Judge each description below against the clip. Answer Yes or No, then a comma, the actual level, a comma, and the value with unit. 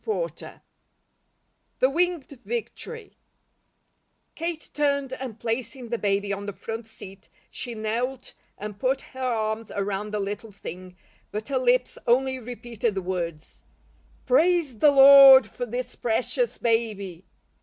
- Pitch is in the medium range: No, high, 235 Hz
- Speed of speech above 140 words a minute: No, slow, 135 wpm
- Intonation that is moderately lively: Yes, average, 4.4 semitones